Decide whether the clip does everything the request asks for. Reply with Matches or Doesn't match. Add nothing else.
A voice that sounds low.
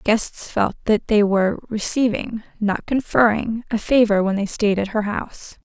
Doesn't match